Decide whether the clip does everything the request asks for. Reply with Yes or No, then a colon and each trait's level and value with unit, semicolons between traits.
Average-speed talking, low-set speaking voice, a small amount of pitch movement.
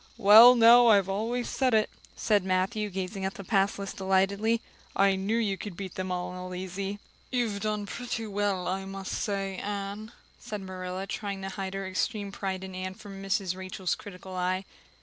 No: average, 180 wpm; high, 195 Hz; narrow, 1.9 semitones